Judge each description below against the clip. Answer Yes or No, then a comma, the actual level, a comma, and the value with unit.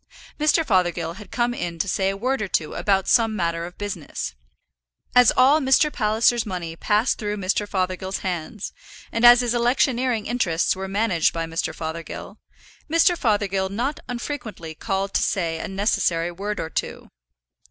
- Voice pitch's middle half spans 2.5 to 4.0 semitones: No, wide, 5.4 semitones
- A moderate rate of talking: Yes, average, 165 wpm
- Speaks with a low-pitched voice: No, high, 200 Hz